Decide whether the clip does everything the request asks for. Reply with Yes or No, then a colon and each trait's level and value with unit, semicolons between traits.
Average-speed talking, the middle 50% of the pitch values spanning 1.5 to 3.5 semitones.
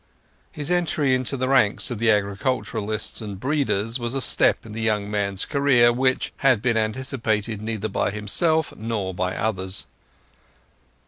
No: average, 150 wpm; average, 3.9 semitones